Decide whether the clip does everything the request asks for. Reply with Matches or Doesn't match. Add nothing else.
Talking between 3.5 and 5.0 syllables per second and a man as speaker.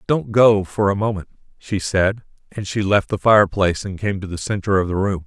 Doesn't match